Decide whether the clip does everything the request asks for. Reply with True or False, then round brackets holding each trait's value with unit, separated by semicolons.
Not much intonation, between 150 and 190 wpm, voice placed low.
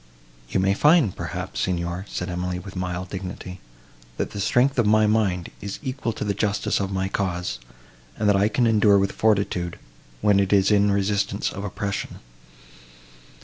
True (2.2 semitones; 170 wpm; 100 Hz)